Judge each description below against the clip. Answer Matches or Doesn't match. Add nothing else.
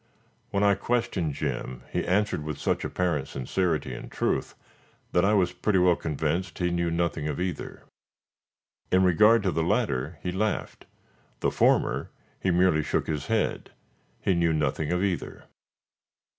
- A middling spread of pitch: Matches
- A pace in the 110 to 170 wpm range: Matches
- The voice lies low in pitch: Matches